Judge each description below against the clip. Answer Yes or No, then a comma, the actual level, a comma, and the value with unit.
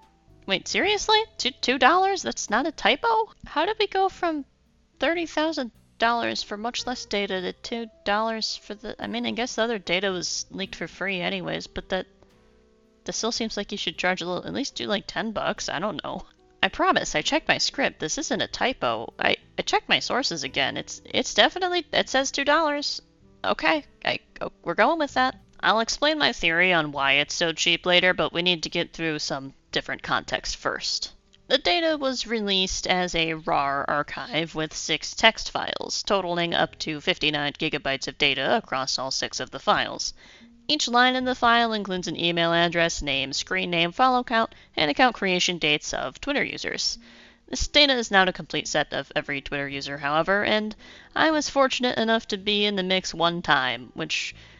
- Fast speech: No, average, 190 wpm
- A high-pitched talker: Yes, high, 195 Hz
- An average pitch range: No, wide, 7.2 semitones